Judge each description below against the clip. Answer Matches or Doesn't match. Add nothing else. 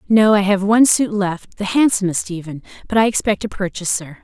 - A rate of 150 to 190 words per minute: Doesn't match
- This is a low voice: Doesn't match